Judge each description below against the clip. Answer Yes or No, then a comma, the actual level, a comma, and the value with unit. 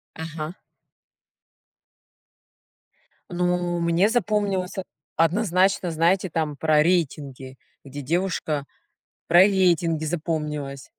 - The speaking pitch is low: No, medium, 170 Hz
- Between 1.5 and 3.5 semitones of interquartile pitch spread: Yes, average, 3.1 semitones